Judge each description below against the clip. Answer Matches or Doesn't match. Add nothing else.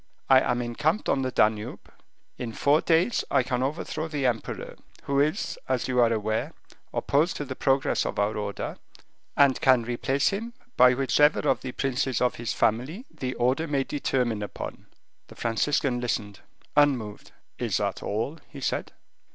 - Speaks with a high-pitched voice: Doesn't match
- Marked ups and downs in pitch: Doesn't match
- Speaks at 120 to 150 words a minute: Doesn't match